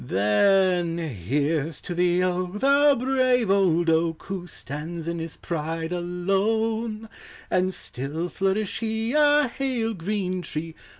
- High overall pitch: No, medium, 180 Hz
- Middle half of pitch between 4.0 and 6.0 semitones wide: Yes, average, 5.1 semitones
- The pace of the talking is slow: Yes, slow, 130 wpm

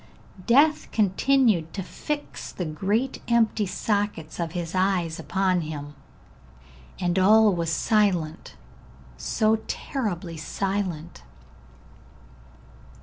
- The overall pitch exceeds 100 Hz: Yes, high, 190 Hz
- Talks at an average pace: No, slow, 90 wpm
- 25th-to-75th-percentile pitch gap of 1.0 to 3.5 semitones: No, average, 4.5 semitones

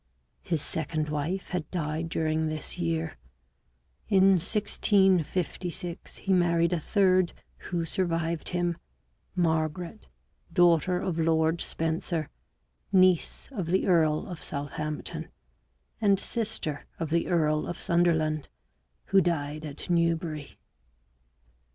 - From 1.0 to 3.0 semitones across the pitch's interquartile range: Yes, narrow, 2.6 semitones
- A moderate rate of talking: No, slow, 110 wpm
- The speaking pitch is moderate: Yes, medium, 170 Hz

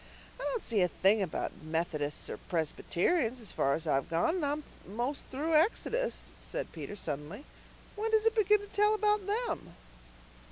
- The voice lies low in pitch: No, very high, 265 Hz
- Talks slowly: No, average, 170 wpm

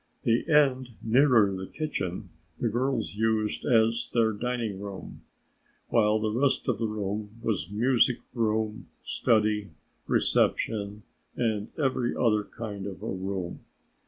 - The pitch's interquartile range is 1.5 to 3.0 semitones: Yes, narrow, 2.6 semitones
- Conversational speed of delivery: No, slow, 130 wpm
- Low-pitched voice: Yes, low, 110 Hz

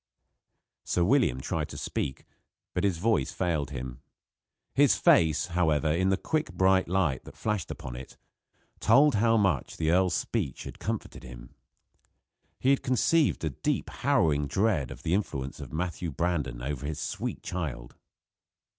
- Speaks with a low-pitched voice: Yes, very low, 85 Hz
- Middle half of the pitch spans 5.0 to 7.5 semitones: Yes, wide, 5.4 semitones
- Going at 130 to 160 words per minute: Yes, average, 155 wpm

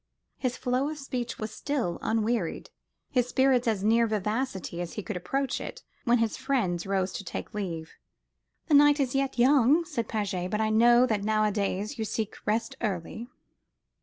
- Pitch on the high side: Yes, high, 225 Hz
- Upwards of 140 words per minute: Yes, average, 170 wpm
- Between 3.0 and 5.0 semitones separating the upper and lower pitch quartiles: Yes, average, 3.8 semitones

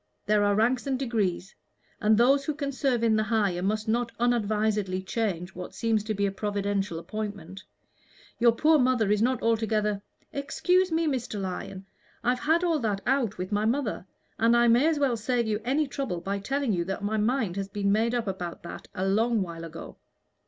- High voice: Yes, high, 220 Hz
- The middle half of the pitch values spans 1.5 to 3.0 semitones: No, average, 3.7 semitones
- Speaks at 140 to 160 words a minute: No, average, 200 wpm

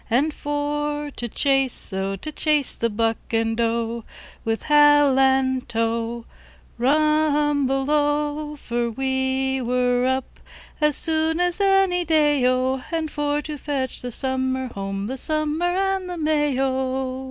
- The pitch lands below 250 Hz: No, very high, 270 Hz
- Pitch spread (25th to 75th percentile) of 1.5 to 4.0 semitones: Yes, average, 3.3 semitones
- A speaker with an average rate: No, slow, 130 wpm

